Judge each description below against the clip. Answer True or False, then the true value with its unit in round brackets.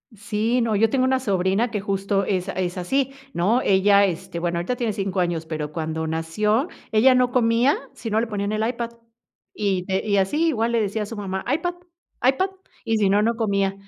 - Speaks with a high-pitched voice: True (210 Hz)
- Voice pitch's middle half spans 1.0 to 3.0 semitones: False (3.7 semitones)